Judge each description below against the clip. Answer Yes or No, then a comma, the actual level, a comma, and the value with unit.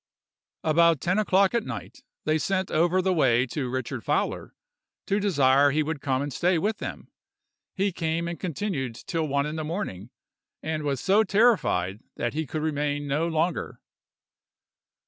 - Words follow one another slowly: No, average, 165 wpm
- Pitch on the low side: No, medium, 160 Hz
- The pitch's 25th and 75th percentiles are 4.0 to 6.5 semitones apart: Yes, average, 4.6 semitones